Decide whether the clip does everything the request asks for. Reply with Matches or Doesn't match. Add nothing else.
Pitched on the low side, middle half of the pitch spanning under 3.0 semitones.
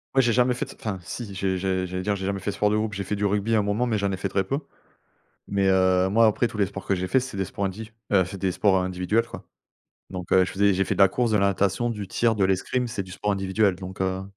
Matches